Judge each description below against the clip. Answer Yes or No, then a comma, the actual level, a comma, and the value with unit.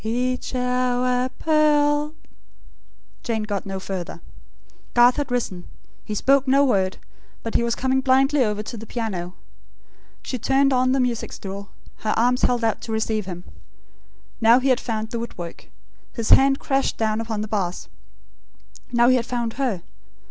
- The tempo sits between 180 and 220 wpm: No, average, 165 wpm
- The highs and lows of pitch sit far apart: No, average, 3.3 semitones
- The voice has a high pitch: Yes, high, 240 Hz